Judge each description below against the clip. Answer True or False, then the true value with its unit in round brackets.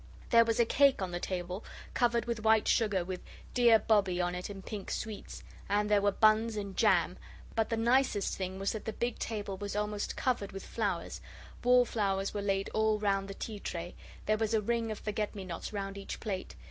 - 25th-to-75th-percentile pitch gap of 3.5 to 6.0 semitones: False (2.4 semitones)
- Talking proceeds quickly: True (210 wpm)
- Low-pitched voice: False (210 Hz)